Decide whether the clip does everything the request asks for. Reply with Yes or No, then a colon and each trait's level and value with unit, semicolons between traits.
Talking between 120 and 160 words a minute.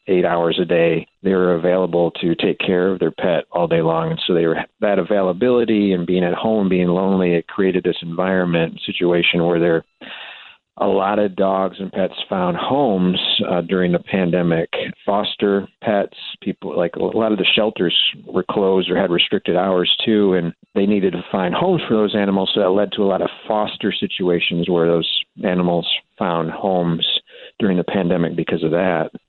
No: average, 190 wpm